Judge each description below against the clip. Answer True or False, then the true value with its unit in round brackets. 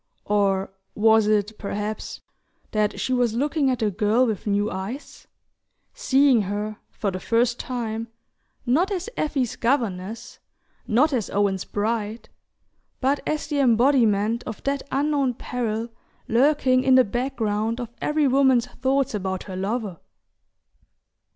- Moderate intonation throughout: True (4.1 semitones)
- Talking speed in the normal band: False (130 wpm)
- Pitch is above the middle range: True (230 Hz)